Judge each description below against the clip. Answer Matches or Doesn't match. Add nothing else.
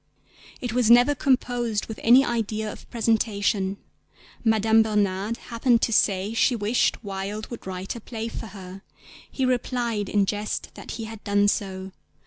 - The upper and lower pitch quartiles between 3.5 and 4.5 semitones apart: Doesn't match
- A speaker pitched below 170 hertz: Doesn't match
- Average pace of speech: Matches